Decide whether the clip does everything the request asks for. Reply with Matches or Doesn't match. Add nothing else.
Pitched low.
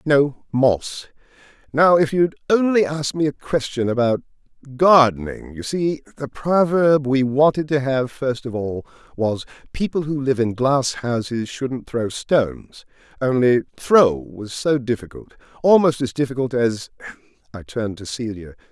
Matches